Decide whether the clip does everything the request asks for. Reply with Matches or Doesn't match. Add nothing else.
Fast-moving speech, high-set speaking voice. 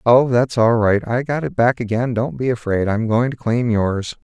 Doesn't match